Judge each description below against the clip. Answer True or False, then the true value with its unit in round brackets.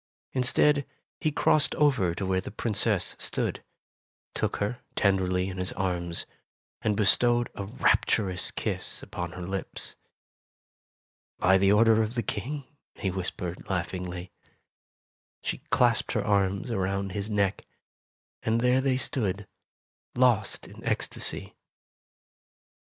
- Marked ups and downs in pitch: False (3.9 semitones)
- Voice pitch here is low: True (100 Hz)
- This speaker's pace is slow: True (125 wpm)